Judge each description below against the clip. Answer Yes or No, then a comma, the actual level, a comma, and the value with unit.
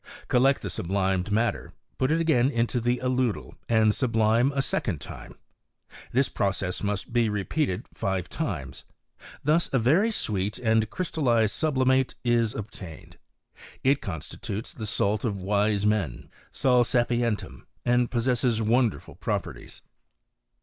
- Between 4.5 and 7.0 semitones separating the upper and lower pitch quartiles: No, average, 3.7 semitones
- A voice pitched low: Yes, low, 115 Hz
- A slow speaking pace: Yes, slow, 130 wpm